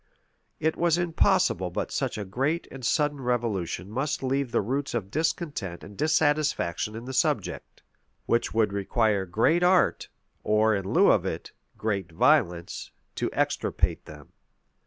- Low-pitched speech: Yes, low, 120 Hz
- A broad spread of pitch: Yes, wide, 7.1 semitones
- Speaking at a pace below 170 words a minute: Yes, average, 150 wpm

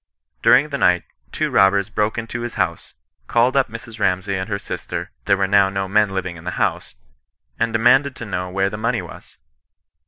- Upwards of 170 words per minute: Yes, average, 190 wpm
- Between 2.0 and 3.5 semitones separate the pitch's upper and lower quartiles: Yes, average, 3.1 semitones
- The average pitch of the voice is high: No, low, 105 Hz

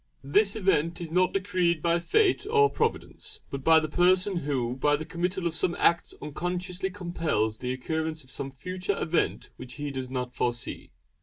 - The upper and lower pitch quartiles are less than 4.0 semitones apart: No, average, 4.7 semitones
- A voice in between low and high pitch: Yes, medium, 170 Hz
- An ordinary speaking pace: Yes, average, 175 wpm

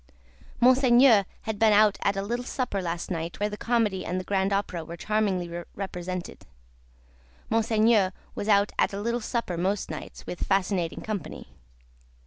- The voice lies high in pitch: Yes, high, 200 Hz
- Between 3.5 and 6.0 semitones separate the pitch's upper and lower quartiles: No, average, 3.1 semitones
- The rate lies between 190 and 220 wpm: No, average, 155 wpm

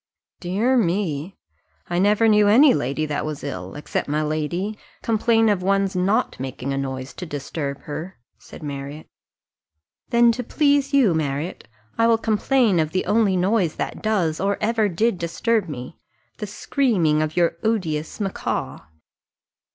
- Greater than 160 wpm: No, average, 150 wpm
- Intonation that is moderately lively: No, wide, 6.3 semitones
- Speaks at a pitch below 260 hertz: Yes, medium, 185 Hz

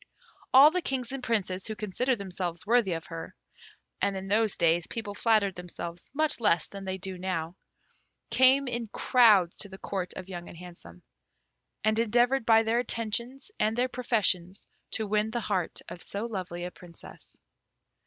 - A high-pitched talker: Yes, high, 205 Hz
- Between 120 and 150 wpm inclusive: No, average, 170 wpm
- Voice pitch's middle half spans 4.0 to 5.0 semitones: Yes, average, 4.6 semitones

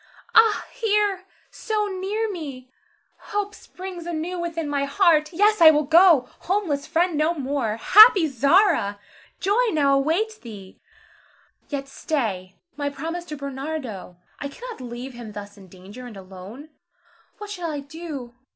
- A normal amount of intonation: No, wide, 6.5 semitones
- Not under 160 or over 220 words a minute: No, average, 140 wpm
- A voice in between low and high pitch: No, very high, 305 Hz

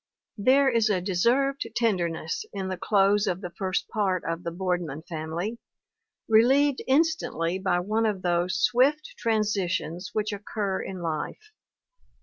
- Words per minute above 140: No, slow, 135 wpm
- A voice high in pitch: Yes, high, 195 Hz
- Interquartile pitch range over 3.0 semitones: Yes, average, 4.4 semitones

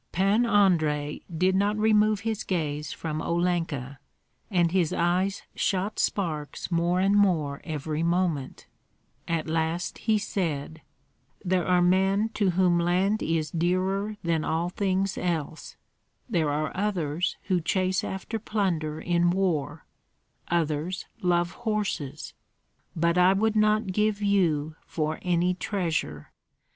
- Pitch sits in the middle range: Yes, medium, 175 Hz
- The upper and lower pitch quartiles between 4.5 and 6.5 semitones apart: No, average, 3.5 semitones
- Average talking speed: No, slow, 125 wpm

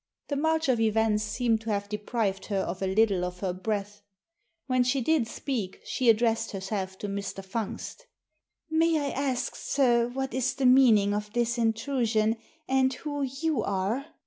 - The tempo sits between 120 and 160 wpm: No, average, 175 wpm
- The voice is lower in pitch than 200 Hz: No, high, 225 Hz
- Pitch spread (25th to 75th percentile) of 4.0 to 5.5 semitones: Yes, average, 4.3 semitones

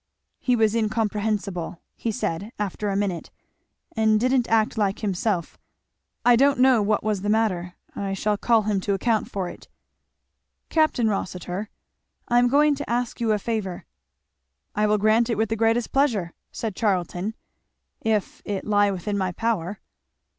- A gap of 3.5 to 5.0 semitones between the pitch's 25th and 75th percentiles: No, narrow, 2.6 semitones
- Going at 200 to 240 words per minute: No, average, 160 wpm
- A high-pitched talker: Yes, high, 215 Hz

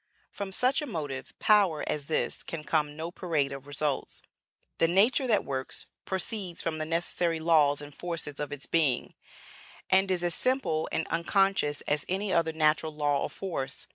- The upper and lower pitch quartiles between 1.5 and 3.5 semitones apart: No, average, 4.3 semitones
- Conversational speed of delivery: Yes, average, 170 wpm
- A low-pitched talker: No, medium, 160 Hz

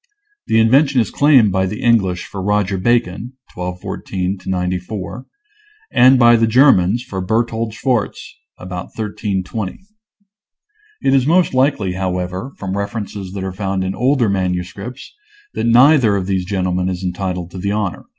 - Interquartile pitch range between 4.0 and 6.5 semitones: Yes, average, 4.3 semitones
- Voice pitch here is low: Yes, low, 100 Hz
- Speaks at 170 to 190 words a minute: No, average, 145 wpm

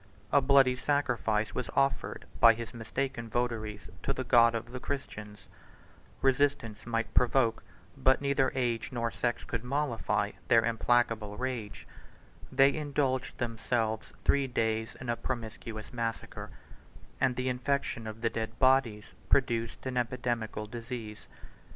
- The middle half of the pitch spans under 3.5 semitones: Yes, narrow, 2.5 semitones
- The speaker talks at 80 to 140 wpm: Yes, slow, 135 wpm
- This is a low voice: Yes, low, 120 Hz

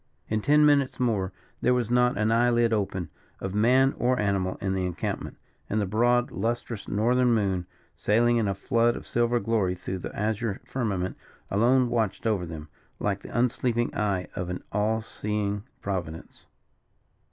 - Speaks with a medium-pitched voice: No, low, 110 Hz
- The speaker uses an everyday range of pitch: Yes, average, 3.5 semitones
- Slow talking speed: No, average, 165 wpm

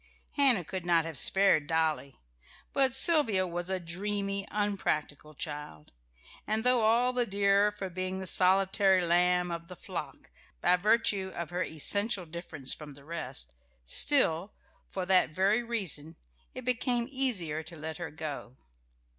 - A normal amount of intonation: Yes, average, 4.3 semitones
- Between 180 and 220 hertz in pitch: Yes, medium, 185 Hz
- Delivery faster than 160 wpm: No, average, 145 wpm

